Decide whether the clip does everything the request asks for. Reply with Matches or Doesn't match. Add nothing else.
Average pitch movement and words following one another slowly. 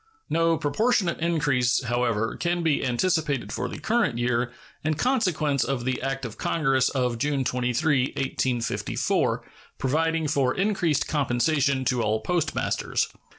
Matches